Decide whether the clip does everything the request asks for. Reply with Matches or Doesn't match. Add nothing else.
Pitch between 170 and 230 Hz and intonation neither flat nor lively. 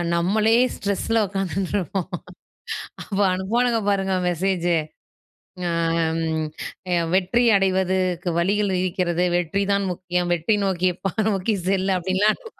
Doesn't match